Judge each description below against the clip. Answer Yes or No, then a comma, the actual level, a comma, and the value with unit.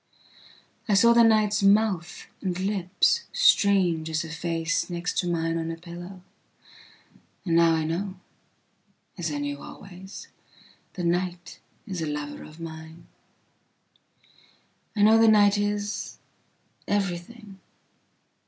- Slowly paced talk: Yes, slow, 115 wpm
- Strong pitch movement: No, average, 3.7 semitones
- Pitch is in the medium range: Yes, medium, 180 Hz